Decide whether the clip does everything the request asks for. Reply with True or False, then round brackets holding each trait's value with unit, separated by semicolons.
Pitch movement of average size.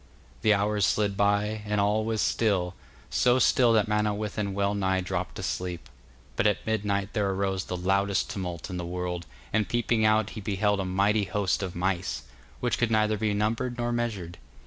False (2.3 semitones)